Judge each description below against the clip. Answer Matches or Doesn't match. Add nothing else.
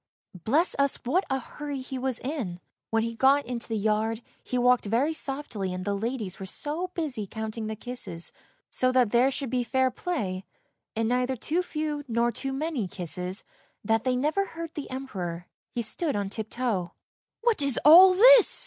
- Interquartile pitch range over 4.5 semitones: Matches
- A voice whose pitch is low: Doesn't match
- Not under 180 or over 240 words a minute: Matches